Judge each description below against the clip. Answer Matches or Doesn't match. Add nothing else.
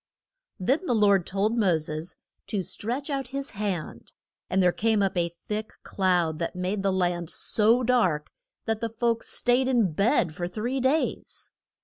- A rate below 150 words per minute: Doesn't match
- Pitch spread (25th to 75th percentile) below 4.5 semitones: Doesn't match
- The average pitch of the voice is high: Matches